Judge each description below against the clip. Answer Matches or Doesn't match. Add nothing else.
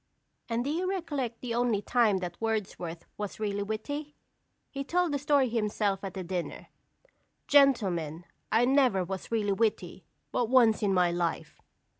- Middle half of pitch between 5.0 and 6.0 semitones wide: Matches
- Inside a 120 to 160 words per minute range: Matches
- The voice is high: Matches